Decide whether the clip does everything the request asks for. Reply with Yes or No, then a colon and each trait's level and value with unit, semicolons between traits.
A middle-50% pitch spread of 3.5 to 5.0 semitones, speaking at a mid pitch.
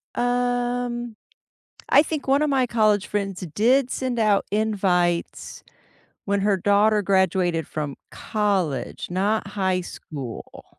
No: average, 4.4 semitones; high, 205 Hz